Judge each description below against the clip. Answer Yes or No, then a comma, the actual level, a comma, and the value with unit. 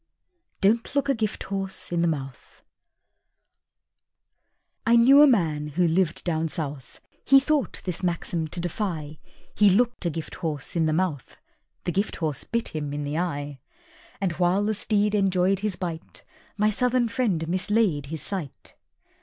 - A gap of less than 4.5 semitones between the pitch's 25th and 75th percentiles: No, average, 5.0 semitones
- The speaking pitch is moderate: Yes, medium, 180 Hz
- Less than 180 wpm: Yes, average, 155 wpm